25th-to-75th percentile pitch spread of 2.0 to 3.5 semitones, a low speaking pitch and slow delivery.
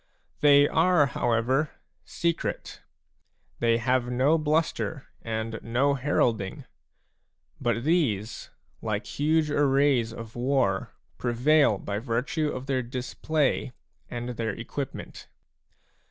No: average, 4.0 semitones; low, 130 Hz; slow, 100 wpm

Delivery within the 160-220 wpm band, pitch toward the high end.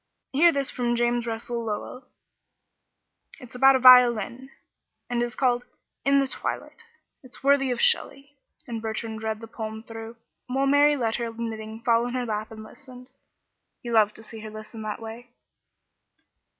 Yes: average, 165 wpm; high, 240 Hz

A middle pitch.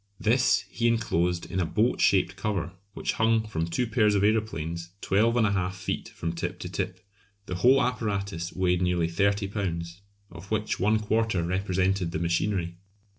No: very low, 95 Hz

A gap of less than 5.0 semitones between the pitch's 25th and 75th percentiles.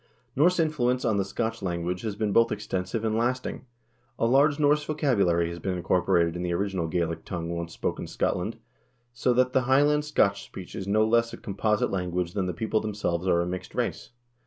No: wide, 5.5 semitones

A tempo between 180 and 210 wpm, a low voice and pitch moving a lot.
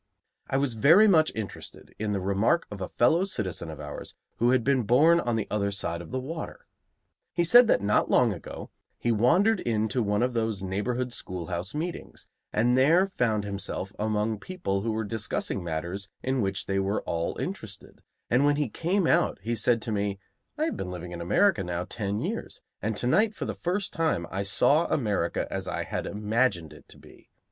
Yes: average, 200 wpm; low, 110 Hz; wide, 6.4 semitones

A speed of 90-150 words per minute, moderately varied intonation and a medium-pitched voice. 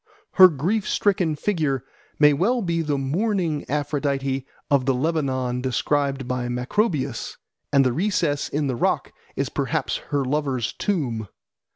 Yes: average, 140 wpm; average, 4.1 semitones; medium, 145 Hz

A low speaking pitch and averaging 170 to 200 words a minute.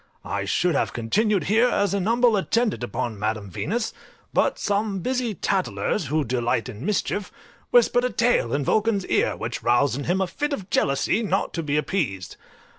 No: medium, 185 Hz; average, 180 wpm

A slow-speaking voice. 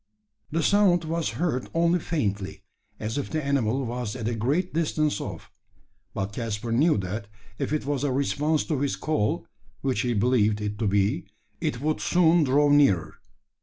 No: average, 170 wpm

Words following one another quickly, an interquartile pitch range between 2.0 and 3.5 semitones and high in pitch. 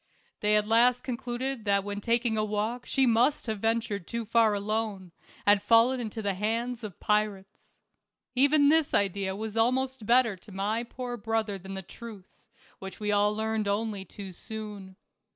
No: average, 170 wpm; narrow, 2.6 semitones; high, 220 Hz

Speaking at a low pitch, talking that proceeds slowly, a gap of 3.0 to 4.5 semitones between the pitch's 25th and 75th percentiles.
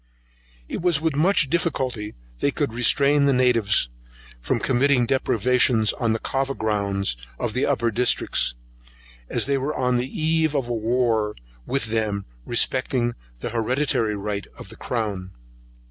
No: low, 120 Hz; average, 145 wpm; average, 4.0 semitones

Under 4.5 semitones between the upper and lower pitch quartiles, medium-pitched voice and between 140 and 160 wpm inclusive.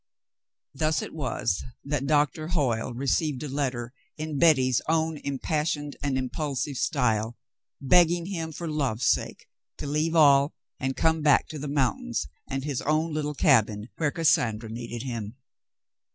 Yes: average, 3.5 semitones; medium, 145 Hz; average, 145 wpm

